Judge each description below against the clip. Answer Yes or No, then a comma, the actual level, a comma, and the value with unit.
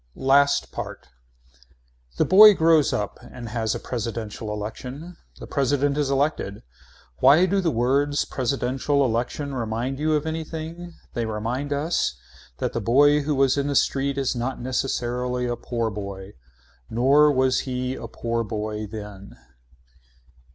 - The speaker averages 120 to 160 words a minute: Yes, average, 145 wpm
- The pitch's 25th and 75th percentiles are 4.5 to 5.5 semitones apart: No, average, 3.8 semitones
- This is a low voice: Yes, low, 130 Hz